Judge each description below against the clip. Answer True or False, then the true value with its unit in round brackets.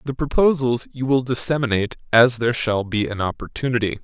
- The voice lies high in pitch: False (120 Hz)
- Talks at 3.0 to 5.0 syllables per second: False (5.9 syllables/s)